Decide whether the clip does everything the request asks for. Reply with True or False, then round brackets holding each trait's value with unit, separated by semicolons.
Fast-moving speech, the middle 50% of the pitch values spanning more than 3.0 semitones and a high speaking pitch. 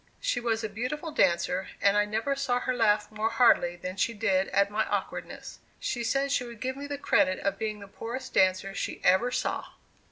True (210 wpm; 4.0 semitones; 220 Hz)